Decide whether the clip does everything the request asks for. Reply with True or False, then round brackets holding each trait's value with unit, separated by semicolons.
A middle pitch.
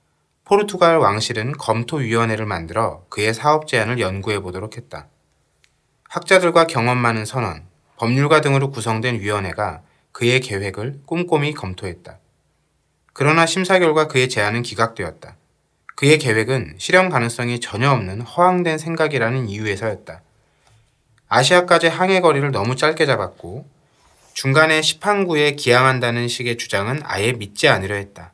False (125 Hz)